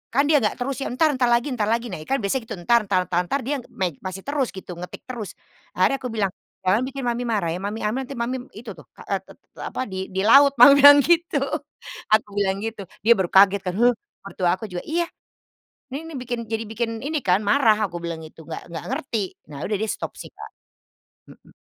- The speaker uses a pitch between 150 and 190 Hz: No, high, 225 Hz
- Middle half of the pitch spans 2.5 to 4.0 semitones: No, average, 5.2 semitones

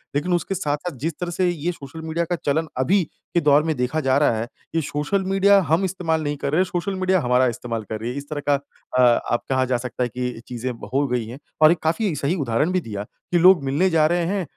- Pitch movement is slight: No, wide, 5.4 semitones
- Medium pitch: Yes, medium, 150 Hz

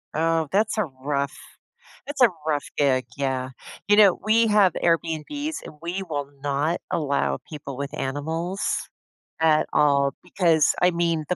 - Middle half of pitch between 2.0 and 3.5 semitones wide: No, average, 4.2 semitones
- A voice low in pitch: No, medium, 160 Hz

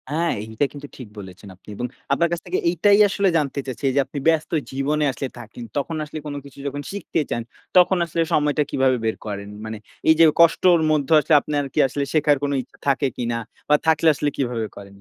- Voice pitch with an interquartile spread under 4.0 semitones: No, average, 4.4 semitones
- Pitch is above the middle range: No, medium, 145 Hz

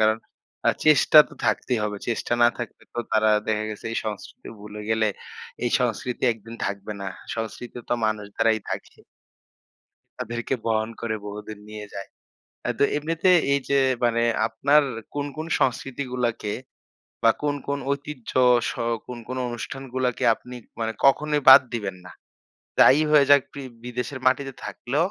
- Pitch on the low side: Yes, low, 120 Hz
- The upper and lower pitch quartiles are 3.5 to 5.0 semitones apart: Yes, average, 3.9 semitones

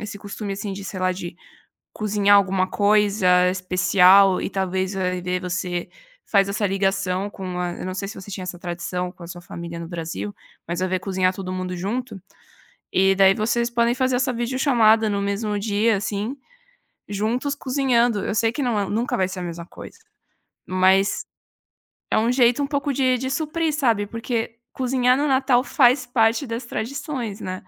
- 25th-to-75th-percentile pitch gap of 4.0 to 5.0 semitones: Yes, average, 4.4 semitones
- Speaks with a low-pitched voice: No, high, 205 Hz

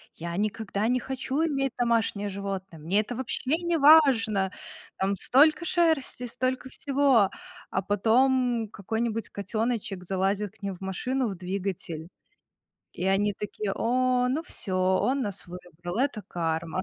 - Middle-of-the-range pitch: No, high, 215 Hz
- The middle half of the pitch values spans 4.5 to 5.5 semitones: Yes, average, 5.0 semitones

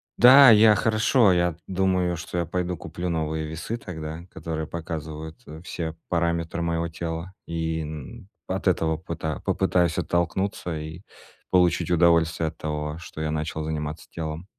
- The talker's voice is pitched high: No, very low, 85 Hz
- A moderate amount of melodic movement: No, narrow, 2.2 semitones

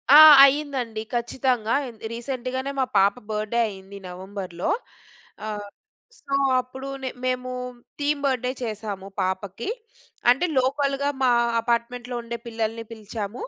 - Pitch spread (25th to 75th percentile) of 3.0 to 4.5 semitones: Yes, average, 3.7 semitones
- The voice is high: Yes, high, 235 Hz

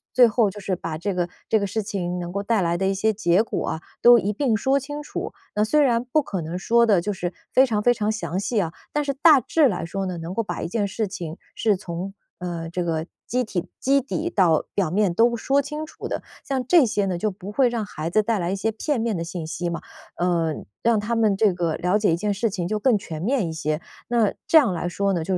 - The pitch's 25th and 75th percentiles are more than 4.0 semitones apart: Yes, average, 5.0 semitones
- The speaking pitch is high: Yes, high, 205 Hz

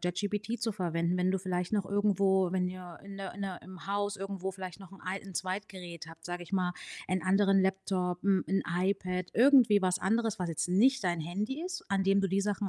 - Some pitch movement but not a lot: No, narrow, 1.8 semitones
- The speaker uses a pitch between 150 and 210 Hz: Yes, high, 190 Hz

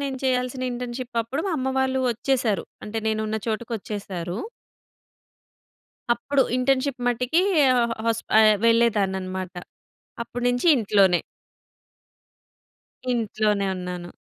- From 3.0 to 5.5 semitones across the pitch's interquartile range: Yes, average, 3.4 semitones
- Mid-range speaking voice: No, high, 230 Hz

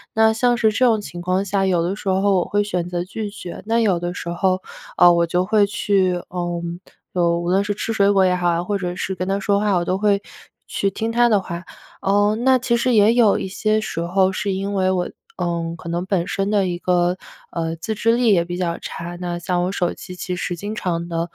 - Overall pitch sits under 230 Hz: Yes, high, 190 Hz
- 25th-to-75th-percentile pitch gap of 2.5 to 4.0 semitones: Yes, average, 2.8 semitones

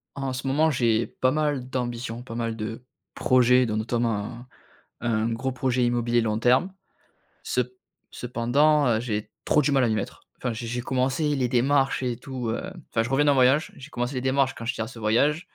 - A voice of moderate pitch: No, low, 125 Hz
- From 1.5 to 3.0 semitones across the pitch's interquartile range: Yes, narrow, 2.5 semitones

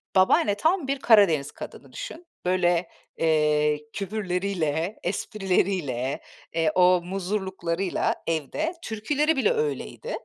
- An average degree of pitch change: Yes, average, 4.9 semitones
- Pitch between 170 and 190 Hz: Yes, medium, 185 Hz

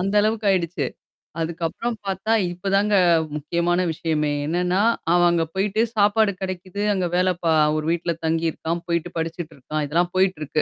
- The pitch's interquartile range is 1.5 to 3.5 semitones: Yes, average, 3.0 semitones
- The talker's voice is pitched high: No, medium, 175 Hz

